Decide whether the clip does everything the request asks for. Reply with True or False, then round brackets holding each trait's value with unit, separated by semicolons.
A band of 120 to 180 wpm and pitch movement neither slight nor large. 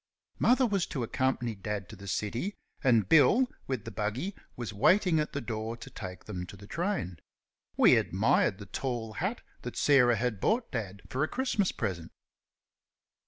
False (170 wpm; 7.2 semitones)